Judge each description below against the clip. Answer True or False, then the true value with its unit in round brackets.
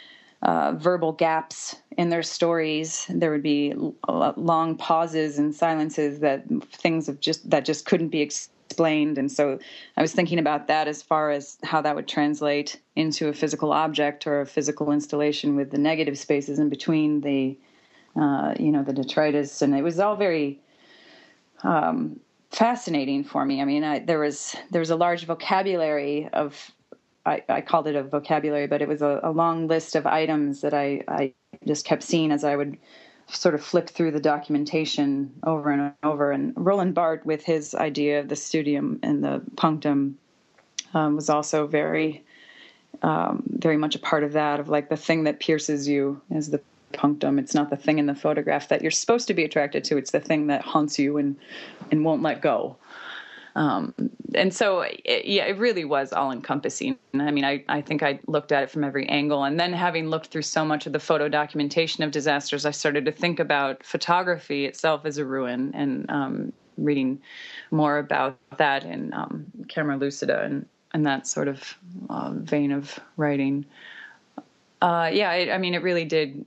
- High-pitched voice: False (150 Hz)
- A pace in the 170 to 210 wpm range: True (190 wpm)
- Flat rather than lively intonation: True (2.1 semitones)